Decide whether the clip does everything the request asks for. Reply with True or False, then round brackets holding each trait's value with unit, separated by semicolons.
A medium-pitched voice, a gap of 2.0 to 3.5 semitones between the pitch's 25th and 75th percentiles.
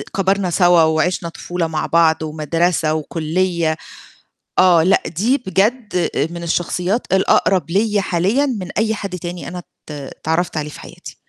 True (175 Hz; 3.0 semitones)